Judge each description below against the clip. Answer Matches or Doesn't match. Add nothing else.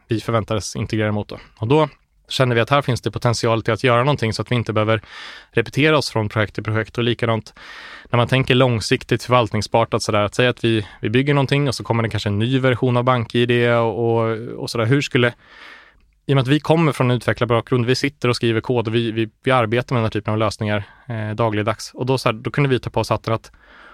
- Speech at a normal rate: Doesn't match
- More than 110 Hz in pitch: Matches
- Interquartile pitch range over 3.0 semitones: Doesn't match